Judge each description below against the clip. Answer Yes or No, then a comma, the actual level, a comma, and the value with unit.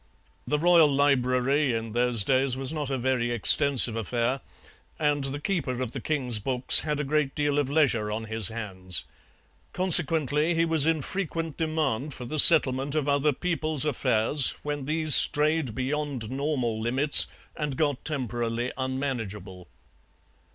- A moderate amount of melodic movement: Yes, average, 3.8 semitones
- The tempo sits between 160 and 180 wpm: No, average, 150 wpm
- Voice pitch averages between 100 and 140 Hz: Yes, low, 135 Hz